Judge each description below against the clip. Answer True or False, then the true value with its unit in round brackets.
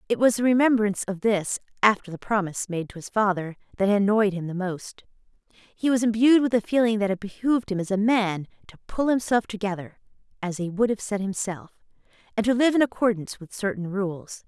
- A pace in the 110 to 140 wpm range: False (205 wpm)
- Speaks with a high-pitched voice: True (205 Hz)